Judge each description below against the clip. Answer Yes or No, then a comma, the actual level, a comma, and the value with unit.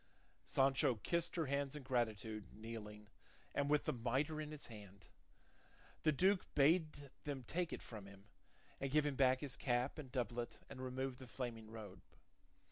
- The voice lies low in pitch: Yes, low, 130 Hz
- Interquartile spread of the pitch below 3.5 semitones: No, average, 4.3 semitones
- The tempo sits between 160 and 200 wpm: Yes, average, 165 wpm